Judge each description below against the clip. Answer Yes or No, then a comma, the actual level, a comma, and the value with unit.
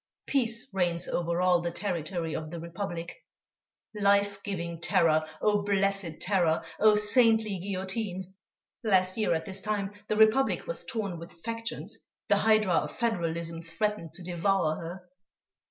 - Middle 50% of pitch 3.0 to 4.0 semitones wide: Yes, average, 3.7 semitones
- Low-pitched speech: No, high, 190 Hz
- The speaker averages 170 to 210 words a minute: No, average, 140 wpm